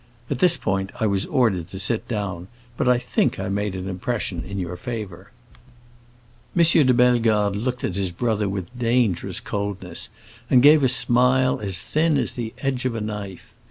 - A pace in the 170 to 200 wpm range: Yes, average, 180 wpm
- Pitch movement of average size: Yes, average, 4.5 semitones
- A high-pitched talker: No, low, 110 Hz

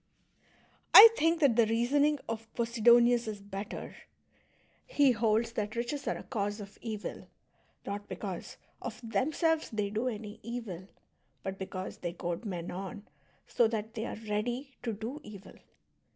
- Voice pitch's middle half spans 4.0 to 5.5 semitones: No, average, 2.8 semitones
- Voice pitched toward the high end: Yes, high, 225 Hz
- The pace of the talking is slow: No, average, 150 wpm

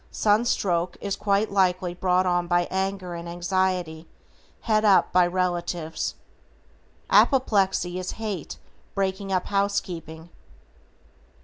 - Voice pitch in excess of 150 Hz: Yes, medium, 185 Hz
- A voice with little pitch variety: Yes, narrow, 2.2 semitones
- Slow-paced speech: Yes, slow, 105 wpm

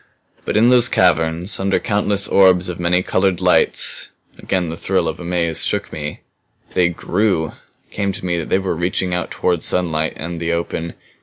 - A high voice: No, very low, 90 Hz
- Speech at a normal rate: Yes, average, 180 wpm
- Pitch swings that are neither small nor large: No, narrow, 2.2 semitones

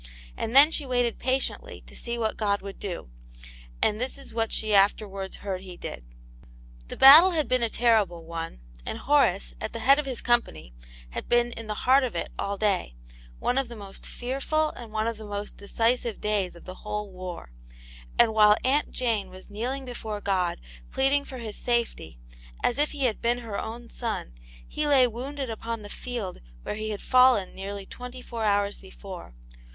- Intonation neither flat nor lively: Yes, average, 3.8 semitones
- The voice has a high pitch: Yes, high, 225 Hz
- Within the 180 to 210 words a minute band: Yes, average, 190 wpm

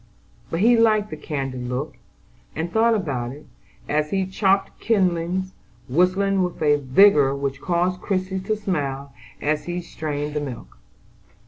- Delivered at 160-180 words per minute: No, average, 145 wpm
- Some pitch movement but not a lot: Yes, average, 5.0 semitones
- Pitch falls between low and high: Yes, medium, 170 Hz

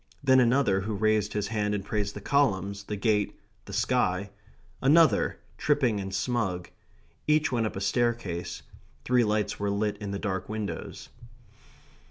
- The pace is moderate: Yes, average, 155 wpm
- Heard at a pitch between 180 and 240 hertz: No, low, 105 Hz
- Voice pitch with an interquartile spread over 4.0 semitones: No, average, 3.2 semitones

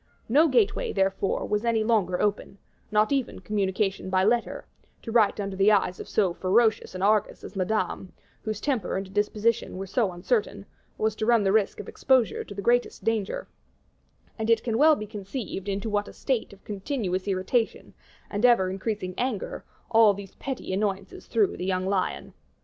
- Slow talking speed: No, average, 180 wpm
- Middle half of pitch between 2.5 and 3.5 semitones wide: Yes, average, 2.8 semitones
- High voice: Yes, high, 210 Hz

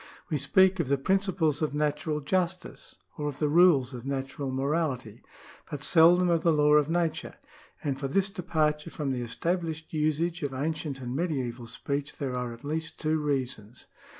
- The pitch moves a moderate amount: Yes, average, 3.5 semitones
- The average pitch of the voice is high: No, medium, 150 Hz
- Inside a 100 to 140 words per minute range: No, average, 180 wpm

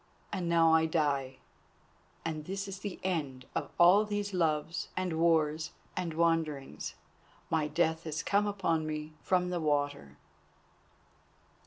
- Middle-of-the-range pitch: Yes, medium, 165 Hz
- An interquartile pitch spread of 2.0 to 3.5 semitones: Yes, average, 2.9 semitones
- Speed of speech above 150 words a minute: No, slow, 135 wpm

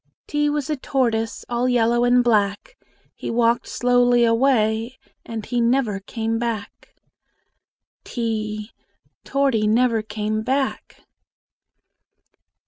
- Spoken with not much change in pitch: Yes, narrow, 2.3 semitones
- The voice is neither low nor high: No, high, 235 Hz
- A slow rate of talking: Yes, slow, 105 wpm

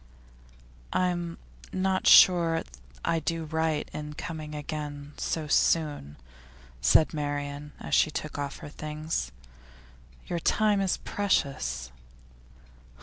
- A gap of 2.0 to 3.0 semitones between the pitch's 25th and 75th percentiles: Yes, narrow, 2.5 semitones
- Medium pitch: Yes, medium, 155 Hz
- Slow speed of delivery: Yes, slow, 110 wpm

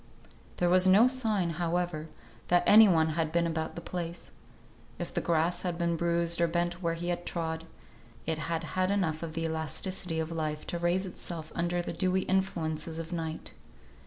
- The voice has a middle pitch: Yes, medium, 170 Hz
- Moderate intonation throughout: No, narrow, 1.6 semitones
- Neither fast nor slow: Yes, average, 185 wpm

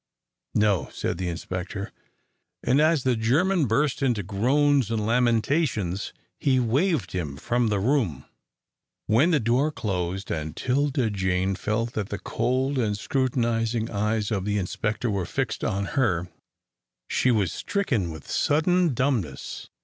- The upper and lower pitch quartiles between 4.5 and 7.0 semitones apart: Yes, average, 5.2 semitones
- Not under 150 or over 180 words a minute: No, average, 140 wpm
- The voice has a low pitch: Yes, low, 115 Hz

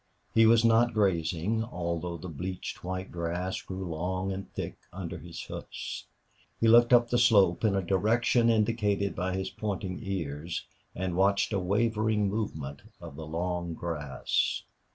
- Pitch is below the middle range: Yes, very low, 95 Hz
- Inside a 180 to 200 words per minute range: No, average, 155 wpm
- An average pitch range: Yes, average, 4.0 semitones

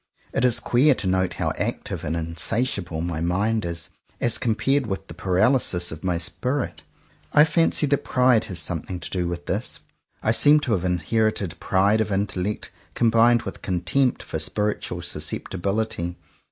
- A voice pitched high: No, low, 100 Hz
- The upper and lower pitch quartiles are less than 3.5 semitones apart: No, average, 5.1 semitones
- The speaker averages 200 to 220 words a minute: No, average, 160 wpm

